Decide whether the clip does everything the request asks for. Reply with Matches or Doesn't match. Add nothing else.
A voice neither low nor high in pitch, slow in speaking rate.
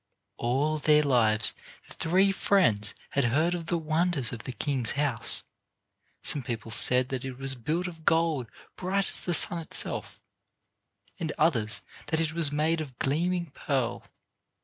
Doesn't match